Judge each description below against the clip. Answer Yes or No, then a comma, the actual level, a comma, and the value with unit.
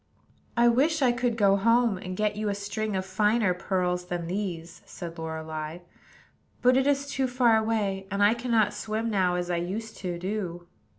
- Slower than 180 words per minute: No, average, 185 wpm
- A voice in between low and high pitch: No, high, 205 Hz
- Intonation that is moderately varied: Yes, average, 4.3 semitones